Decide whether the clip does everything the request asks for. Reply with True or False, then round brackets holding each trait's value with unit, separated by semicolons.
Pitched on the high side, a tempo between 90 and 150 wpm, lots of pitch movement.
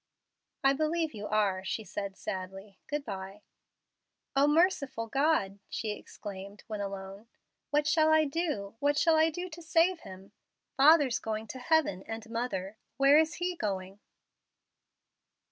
True (230 Hz; 145 wpm; 7.7 semitones)